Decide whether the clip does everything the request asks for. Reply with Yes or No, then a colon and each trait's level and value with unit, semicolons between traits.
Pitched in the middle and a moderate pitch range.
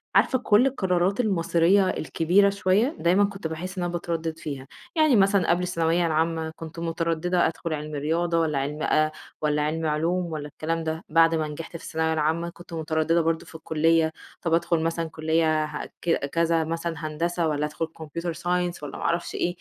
No: medium, 165 Hz; narrow, 1.7 semitones